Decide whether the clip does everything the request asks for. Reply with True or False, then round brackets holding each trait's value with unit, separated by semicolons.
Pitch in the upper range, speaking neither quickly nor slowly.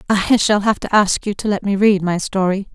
False (200 Hz; 260 wpm)